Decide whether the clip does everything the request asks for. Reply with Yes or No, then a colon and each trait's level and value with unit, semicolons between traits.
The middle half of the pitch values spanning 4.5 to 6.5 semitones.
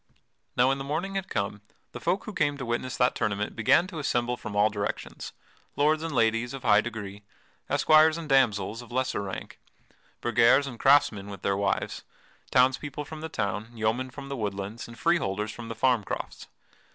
Yes: average, 5.1 semitones